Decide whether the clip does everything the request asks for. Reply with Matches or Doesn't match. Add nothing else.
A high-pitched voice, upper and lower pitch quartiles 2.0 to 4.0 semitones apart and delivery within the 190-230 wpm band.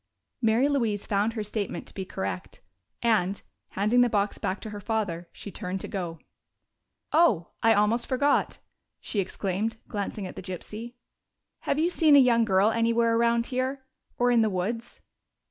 Doesn't match